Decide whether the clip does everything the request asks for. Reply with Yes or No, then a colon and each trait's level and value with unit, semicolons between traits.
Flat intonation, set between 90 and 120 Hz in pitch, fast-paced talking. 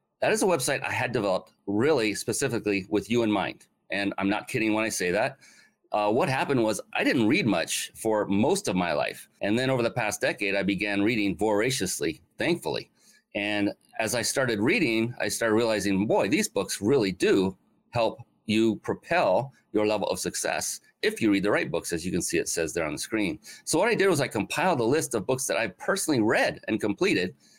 Yes: narrow, 2.0 semitones; low, 105 Hz; fast, 215 wpm